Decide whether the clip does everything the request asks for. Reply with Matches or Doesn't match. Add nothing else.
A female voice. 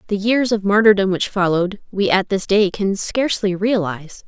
Matches